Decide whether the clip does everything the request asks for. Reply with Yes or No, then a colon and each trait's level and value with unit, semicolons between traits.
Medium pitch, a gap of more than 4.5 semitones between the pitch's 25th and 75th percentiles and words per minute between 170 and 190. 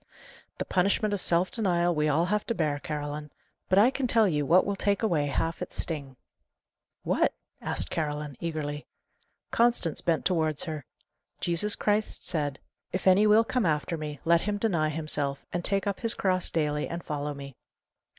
Yes: medium, 170 Hz; average, 5.0 semitones; average, 175 wpm